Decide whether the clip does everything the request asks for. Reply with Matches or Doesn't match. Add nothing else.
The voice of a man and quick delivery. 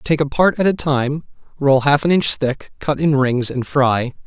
Matches